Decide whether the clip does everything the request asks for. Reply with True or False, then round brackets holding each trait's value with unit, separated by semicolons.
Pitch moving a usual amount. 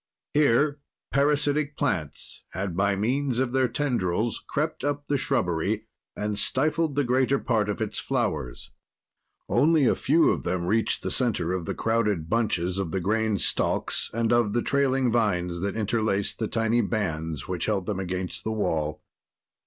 False (6.2 semitones)